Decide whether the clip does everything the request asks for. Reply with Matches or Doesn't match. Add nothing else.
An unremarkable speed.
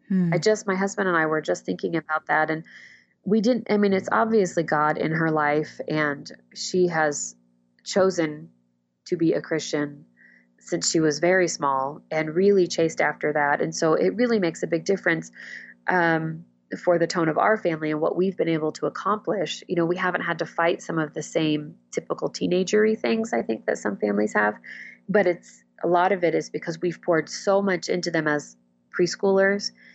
Matches